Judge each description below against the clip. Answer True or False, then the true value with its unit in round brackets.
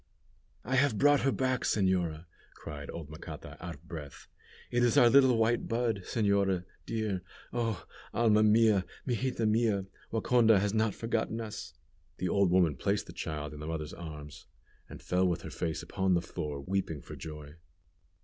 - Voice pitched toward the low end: True (100 Hz)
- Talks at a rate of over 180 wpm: False (170 wpm)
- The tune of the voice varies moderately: False (5.7 semitones)